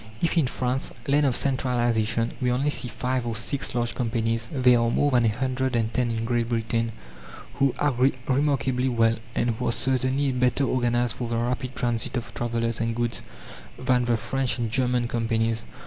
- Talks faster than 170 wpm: Yes, average, 185 wpm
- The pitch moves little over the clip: Yes, narrow, 1.9 semitones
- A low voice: Yes, low, 120 Hz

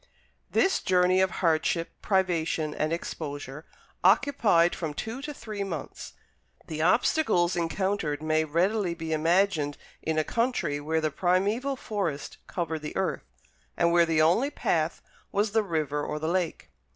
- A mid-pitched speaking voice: Yes, medium, 170 Hz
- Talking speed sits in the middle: Yes, average, 145 wpm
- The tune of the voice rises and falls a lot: No, average, 4.2 semitones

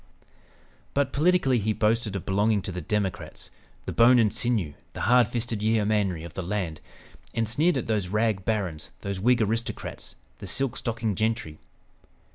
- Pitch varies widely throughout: No, average, 3.2 semitones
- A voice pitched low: Yes, low, 110 Hz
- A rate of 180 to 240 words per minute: No, average, 160 wpm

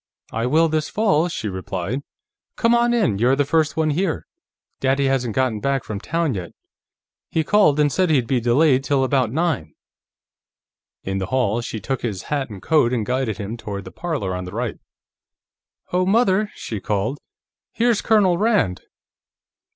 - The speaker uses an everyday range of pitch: No, wide, 6.9 semitones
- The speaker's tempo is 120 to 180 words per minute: Yes, average, 170 wpm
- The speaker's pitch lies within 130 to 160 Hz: Yes, low, 135 Hz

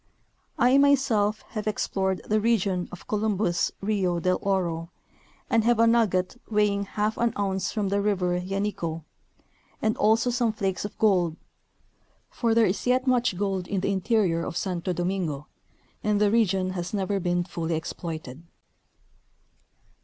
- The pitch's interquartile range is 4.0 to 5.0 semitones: No, average, 3.4 semitones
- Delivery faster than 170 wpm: No, average, 145 wpm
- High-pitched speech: Yes, high, 200 Hz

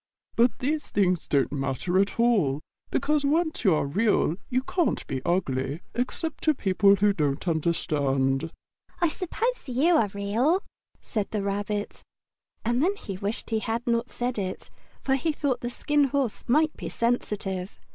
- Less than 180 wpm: Yes, average, 160 wpm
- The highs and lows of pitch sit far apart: Yes, wide, 6.9 semitones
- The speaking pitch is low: No, high, 215 Hz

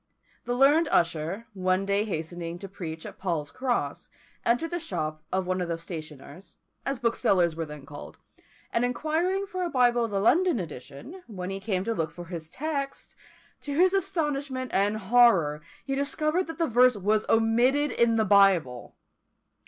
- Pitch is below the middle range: No, high, 215 Hz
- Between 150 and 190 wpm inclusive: Yes, average, 170 wpm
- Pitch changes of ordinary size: No, wide, 8.0 semitones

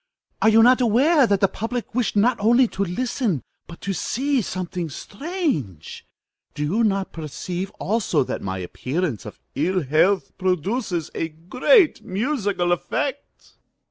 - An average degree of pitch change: No, wide, 6.3 semitones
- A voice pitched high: Yes, high, 200 Hz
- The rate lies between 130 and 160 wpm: Yes, average, 140 wpm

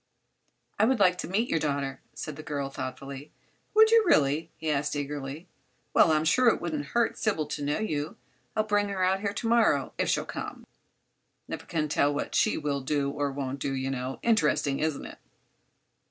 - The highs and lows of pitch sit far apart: Yes, wide, 6.5 semitones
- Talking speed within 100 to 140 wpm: No, average, 195 wpm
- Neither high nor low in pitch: Yes, medium, 150 Hz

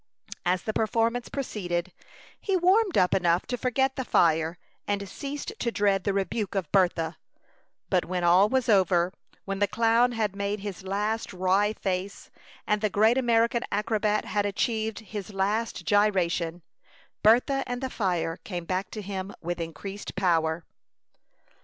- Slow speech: No, average, 155 wpm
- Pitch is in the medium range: No, high, 200 Hz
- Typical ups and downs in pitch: Yes, average, 3.6 semitones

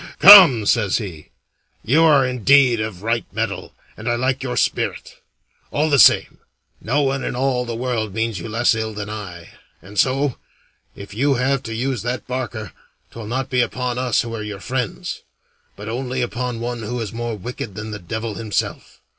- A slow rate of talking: No, average, 185 wpm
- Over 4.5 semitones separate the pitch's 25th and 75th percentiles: No, average, 3.0 semitones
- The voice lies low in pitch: Yes, low, 120 Hz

